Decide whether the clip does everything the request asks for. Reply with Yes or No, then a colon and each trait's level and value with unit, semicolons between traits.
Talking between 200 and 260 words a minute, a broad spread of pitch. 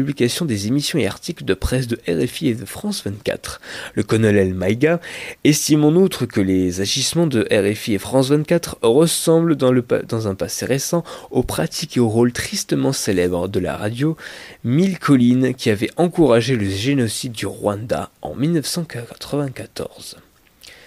No: average, 160 wpm; wide, 6.3 semitones